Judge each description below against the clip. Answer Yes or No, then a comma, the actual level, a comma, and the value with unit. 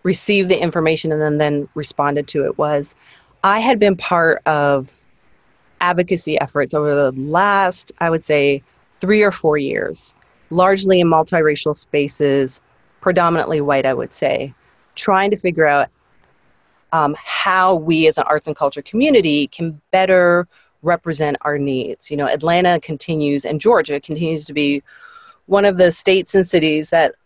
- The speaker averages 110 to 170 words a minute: Yes, average, 155 wpm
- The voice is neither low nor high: Yes, medium, 160 Hz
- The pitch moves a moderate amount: Yes, average, 3.9 semitones